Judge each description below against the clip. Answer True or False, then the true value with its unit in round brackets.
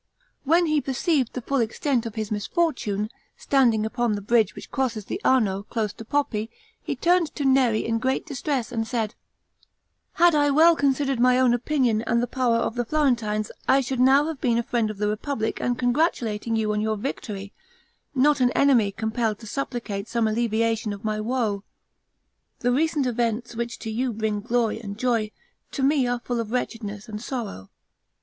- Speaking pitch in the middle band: False (235 Hz)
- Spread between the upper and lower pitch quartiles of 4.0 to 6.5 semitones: False (3.5 semitones)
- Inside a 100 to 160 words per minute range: False (185 wpm)